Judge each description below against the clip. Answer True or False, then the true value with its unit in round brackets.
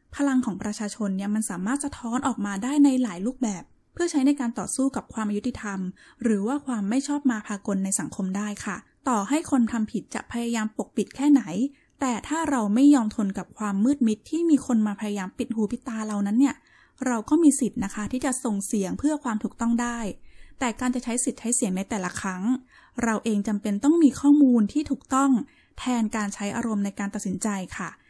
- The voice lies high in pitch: True (230 Hz)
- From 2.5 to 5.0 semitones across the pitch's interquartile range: True (4.1 semitones)